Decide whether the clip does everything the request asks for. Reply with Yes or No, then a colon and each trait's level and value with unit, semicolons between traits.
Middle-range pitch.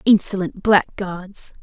No: high, 195 Hz